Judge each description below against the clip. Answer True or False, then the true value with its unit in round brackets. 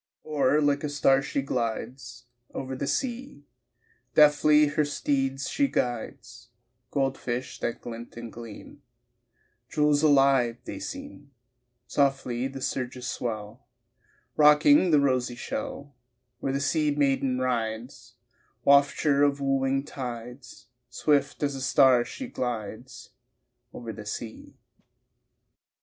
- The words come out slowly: True (115 wpm)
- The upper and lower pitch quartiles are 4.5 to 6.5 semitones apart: False (2.9 semitones)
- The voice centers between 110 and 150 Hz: True (135 Hz)